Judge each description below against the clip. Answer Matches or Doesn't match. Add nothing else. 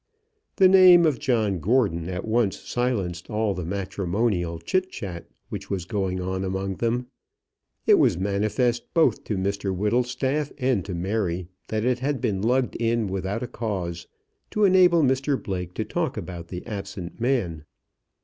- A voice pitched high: Doesn't match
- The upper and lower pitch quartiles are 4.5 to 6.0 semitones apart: Matches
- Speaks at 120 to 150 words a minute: Doesn't match